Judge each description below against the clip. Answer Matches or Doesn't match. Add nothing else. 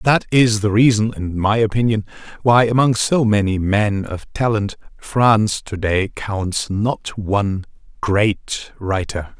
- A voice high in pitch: Doesn't match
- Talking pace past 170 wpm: Doesn't match